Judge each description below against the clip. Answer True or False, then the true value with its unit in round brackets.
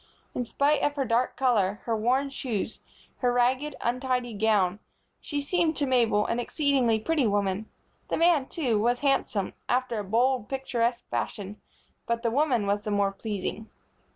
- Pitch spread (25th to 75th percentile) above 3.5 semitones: True (4.0 semitones)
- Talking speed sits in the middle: True (160 wpm)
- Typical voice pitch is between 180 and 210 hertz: False (240 Hz)